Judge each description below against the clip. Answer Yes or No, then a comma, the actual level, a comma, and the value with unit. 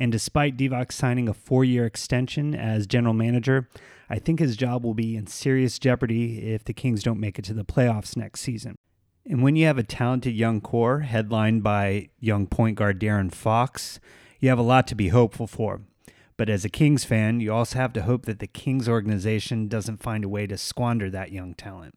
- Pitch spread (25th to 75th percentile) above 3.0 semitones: No, average, 2.7 semitones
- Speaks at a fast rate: Yes, fast, 210 wpm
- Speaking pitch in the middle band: No, low, 115 Hz